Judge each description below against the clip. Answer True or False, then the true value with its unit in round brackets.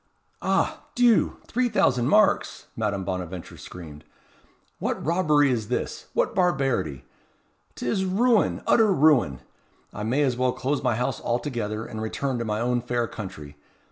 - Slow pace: False (145 wpm)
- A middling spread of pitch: False (6.0 semitones)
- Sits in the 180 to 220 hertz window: False (125 Hz)